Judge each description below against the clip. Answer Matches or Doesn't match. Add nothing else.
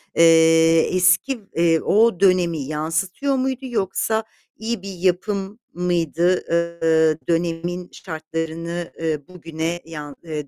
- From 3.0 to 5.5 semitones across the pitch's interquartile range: Doesn't match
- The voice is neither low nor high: Matches